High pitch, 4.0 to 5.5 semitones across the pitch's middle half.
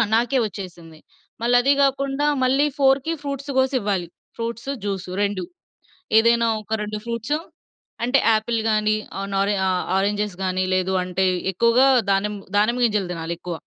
Yes: high, 215 Hz; average, 4.7 semitones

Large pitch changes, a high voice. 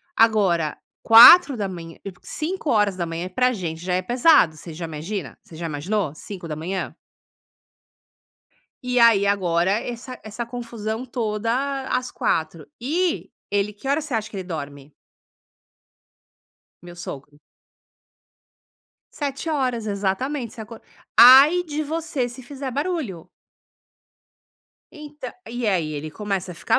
Yes: wide, 6.5 semitones; high, 215 Hz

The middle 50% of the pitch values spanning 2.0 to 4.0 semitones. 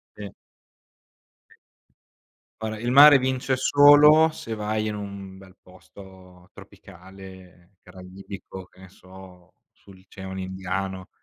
Yes: average, 2.7 semitones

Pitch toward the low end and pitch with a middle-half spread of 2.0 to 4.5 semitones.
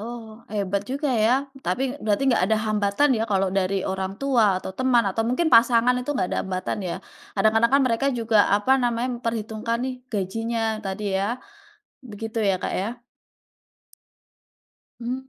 No: high, 225 Hz; average, 3.3 semitones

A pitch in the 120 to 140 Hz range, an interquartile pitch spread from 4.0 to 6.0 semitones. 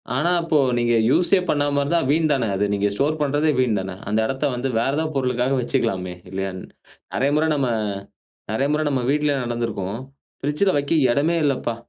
Yes: low, 135 Hz; average, 4.3 semitones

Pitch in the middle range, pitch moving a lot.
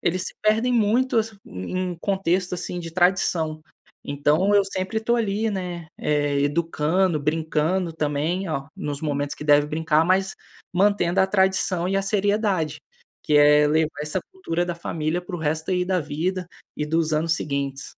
No: medium, 170 Hz; average, 4.0 semitones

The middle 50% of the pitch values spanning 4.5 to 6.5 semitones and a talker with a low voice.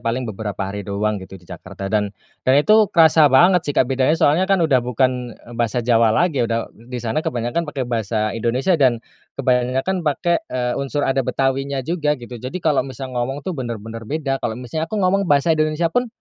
Yes: average, 5.0 semitones; low, 130 Hz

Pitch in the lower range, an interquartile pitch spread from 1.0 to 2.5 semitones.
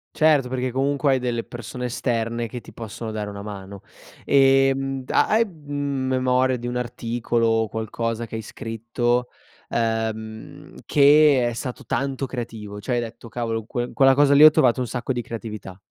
No: low, 120 Hz; average, 2.9 semitones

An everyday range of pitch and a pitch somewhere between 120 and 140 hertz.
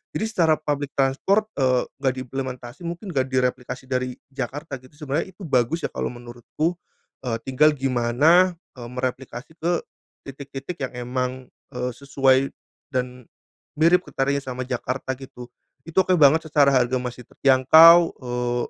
Yes: average, 3.4 semitones; low, 135 Hz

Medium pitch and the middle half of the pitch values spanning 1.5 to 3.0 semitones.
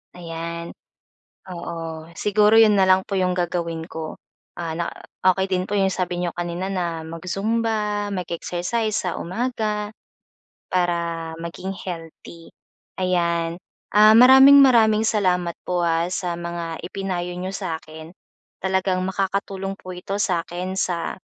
Yes: medium, 180 Hz; average, 2.7 semitones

